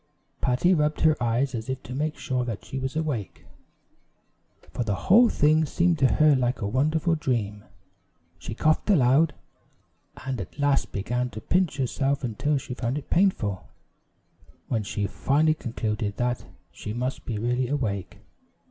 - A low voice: Yes, low, 130 Hz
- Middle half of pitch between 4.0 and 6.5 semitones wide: Yes, average, 4.5 semitones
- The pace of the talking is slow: No, average, 155 wpm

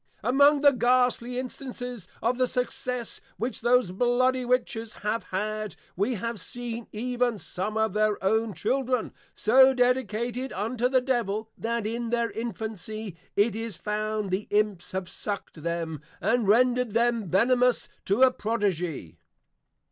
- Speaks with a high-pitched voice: Yes, high, 230 Hz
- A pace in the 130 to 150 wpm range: Yes, average, 140 wpm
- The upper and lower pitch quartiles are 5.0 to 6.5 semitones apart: No, average, 2.9 semitones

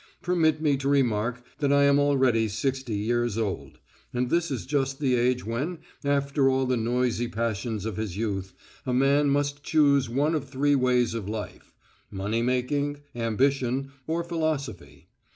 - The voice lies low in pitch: Yes, low, 130 Hz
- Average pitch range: Yes, average, 3.7 semitones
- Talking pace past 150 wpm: Yes, average, 160 wpm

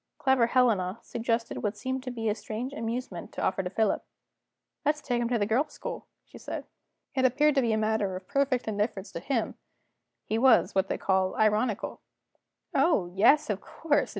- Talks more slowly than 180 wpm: No, average, 185 wpm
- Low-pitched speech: No, high, 230 Hz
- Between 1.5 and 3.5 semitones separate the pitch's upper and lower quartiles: No, average, 4.0 semitones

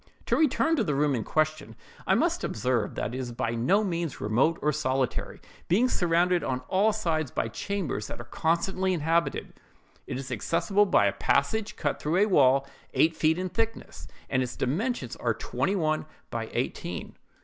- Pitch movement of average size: No, wide, 6.3 semitones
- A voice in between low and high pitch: Yes, medium, 155 Hz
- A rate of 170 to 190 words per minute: Yes, average, 180 wpm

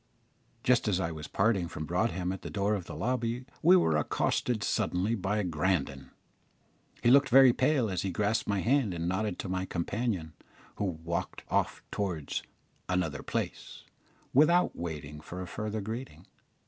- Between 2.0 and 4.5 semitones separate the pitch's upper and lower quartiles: No, average, 5.2 semitones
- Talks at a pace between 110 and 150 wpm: No, average, 160 wpm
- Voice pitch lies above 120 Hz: No, very low, 95 Hz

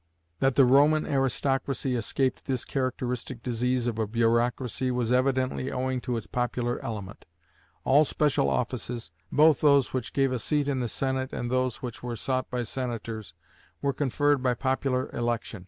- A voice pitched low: Yes, low, 125 Hz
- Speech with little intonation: Yes, narrow, 2.0 semitones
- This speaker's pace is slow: No, average, 160 wpm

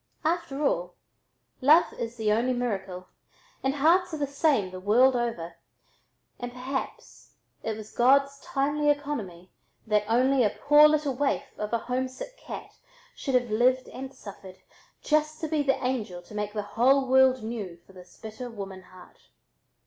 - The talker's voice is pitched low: No, very high, 250 Hz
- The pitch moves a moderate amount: Yes, average, 4.8 semitones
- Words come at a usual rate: Yes, average, 160 wpm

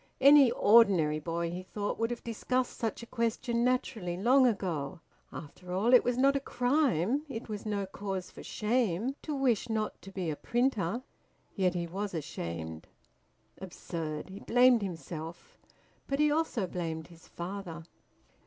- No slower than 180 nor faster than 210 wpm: No, average, 155 wpm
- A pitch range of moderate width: No, wide, 6.1 semitones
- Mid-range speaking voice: No, high, 205 Hz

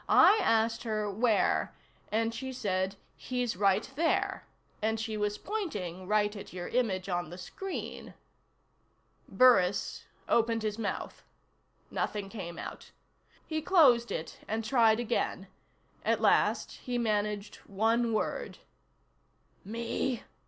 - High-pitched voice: Yes, high, 220 Hz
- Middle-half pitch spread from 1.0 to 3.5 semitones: Yes, average, 3.0 semitones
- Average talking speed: No, slow, 120 wpm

